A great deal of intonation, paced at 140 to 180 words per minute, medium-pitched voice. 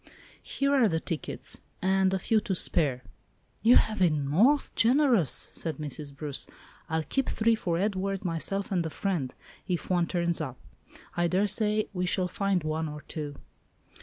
No: average, 4.5 semitones; average, 165 wpm; medium, 180 Hz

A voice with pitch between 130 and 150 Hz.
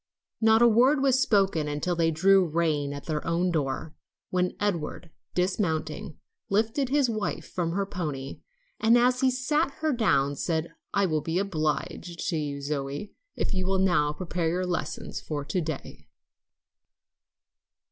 No: medium, 175 Hz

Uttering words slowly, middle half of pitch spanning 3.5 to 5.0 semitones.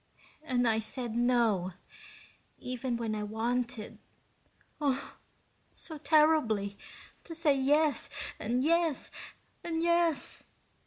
No: slow, 100 wpm; wide, 5.4 semitones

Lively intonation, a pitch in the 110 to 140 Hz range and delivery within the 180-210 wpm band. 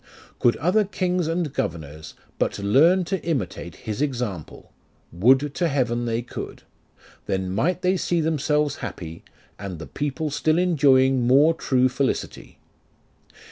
No: wide, 6.8 semitones; low, 135 Hz; average, 140 wpm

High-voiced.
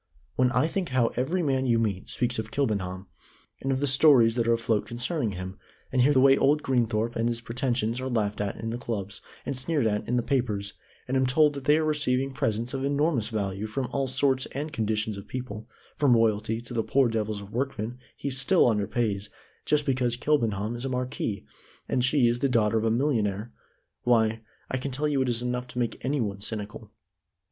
No: low, 120 Hz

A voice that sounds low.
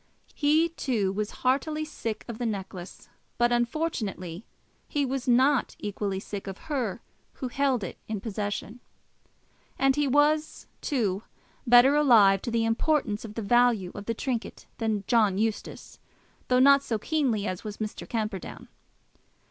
No: high, 230 Hz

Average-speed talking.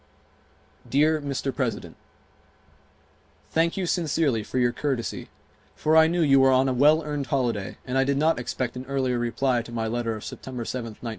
Yes: average, 180 wpm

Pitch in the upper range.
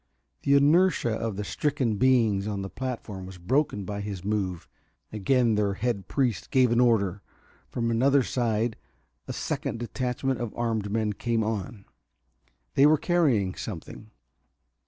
No: low, 115 Hz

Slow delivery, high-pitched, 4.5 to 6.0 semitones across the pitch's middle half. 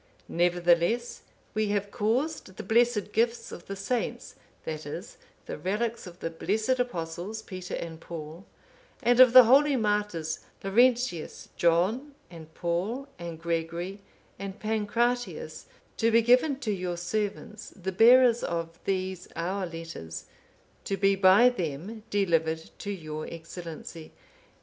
Yes: slow, 130 wpm; high, 195 Hz; average, 5.3 semitones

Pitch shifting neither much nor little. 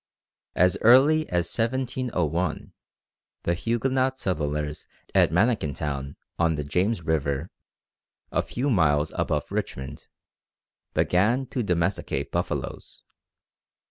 No: wide, 8.0 semitones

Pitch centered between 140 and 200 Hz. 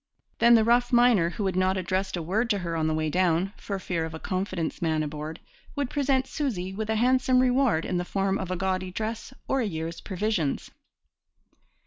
Yes: high, 190 Hz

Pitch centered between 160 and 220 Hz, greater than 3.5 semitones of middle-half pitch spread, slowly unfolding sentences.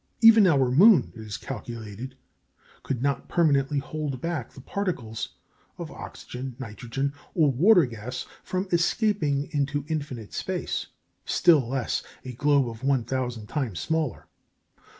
No: low, 135 Hz; average, 4.3 semitones; slow, 130 wpm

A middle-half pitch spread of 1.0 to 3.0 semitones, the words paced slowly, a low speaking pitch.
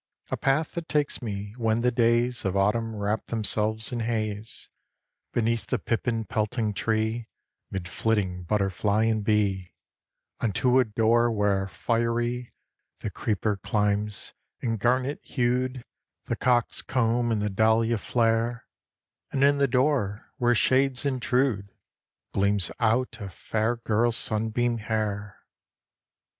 Yes: narrow, 2.6 semitones; slow, 125 wpm; low, 115 Hz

